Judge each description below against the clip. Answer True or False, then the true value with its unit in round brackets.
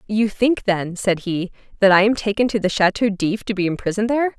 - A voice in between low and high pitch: False (205 Hz)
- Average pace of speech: False (235 wpm)